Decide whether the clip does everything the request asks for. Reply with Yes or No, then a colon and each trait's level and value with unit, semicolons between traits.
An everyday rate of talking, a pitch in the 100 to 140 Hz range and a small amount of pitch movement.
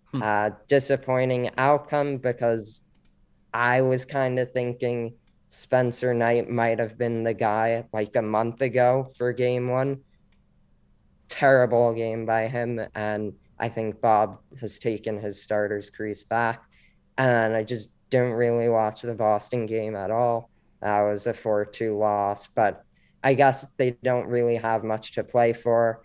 Yes: average, 150 wpm; low, 115 Hz; narrow, 2.3 semitones